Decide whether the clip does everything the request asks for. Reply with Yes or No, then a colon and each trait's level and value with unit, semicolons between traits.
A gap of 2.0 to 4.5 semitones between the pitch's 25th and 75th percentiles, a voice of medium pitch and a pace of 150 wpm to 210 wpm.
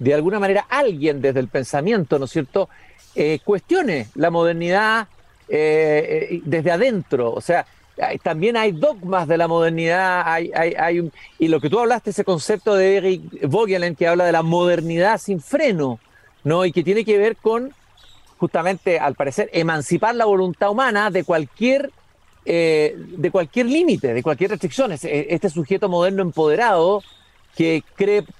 Yes: average, 4.0 semitones; medium, 180 Hz; average, 160 wpm